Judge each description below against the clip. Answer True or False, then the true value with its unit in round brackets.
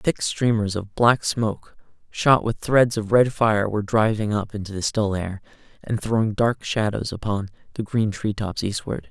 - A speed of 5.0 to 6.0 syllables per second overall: False (4.6 syllables/s)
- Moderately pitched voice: False (110 Hz)